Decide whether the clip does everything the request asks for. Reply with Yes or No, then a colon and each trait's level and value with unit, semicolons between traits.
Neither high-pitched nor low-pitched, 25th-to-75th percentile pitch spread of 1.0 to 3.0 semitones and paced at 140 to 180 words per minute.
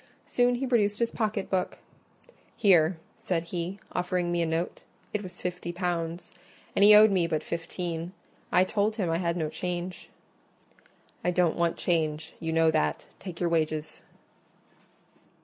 Yes: medium, 175 Hz; narrow, 2.5 semitones; average, 155 wpm